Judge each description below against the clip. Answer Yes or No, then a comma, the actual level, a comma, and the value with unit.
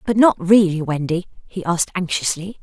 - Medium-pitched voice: Yes, medium, 180 Hz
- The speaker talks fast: No, average, 160 wpm